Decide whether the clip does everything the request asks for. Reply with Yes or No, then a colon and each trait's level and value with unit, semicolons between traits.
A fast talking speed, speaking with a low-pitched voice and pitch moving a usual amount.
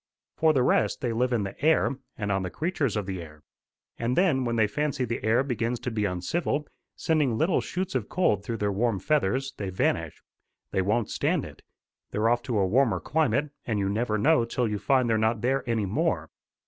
Yes: fast, 210 wpm; low, 115 Hz; average, 4.8 semitones